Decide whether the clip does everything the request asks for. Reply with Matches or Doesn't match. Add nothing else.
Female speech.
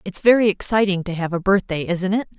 Matches